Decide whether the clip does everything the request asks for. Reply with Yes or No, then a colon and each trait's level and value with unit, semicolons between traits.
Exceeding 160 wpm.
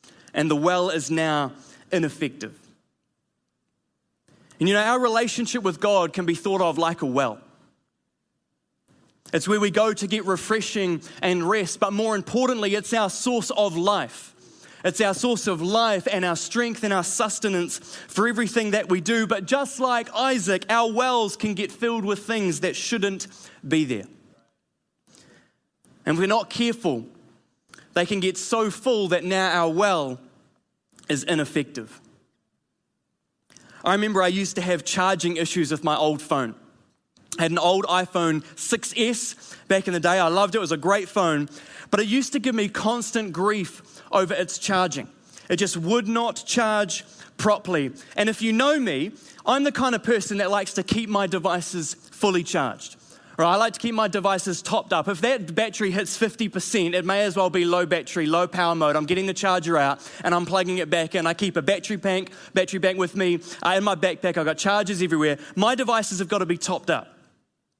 Yes: average, 185 wpm